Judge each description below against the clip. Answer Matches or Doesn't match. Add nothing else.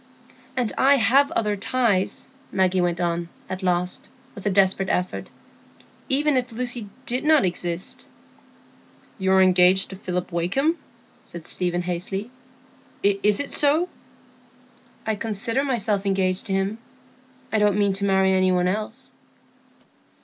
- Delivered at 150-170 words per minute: Doesn't match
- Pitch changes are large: Doesn't match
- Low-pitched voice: Doesn't match